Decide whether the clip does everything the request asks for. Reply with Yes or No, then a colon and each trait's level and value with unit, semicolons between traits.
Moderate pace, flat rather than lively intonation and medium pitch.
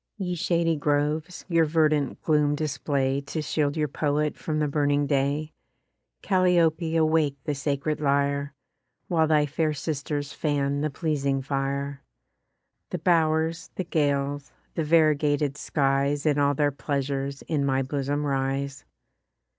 No: slow, 130 wpm; narrow, 1.9 semitones; medium, 145 Hz